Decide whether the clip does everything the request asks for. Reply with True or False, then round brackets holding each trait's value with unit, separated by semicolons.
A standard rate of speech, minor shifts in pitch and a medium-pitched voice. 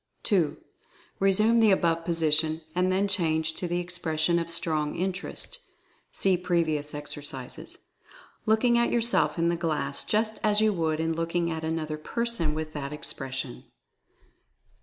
False (150 wpm; 3.5 semitones; 165 Hz)